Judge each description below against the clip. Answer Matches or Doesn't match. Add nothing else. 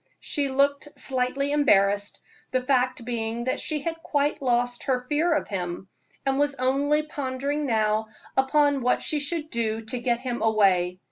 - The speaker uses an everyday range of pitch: Matches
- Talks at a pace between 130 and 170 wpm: Matches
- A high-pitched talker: Matches